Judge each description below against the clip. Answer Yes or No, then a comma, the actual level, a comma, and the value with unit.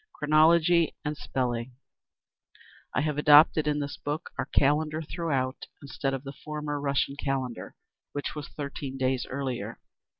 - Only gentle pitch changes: Yes, narrow, 2.1 semitones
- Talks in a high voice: No, medium, 145 Hz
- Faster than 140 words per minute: No, slow, 135 wpm